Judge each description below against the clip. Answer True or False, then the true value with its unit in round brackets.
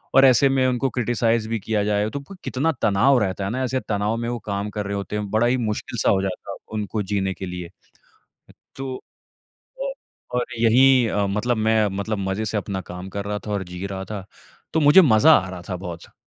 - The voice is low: True (110 Hz)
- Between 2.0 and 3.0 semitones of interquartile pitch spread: False (3.6 semitones)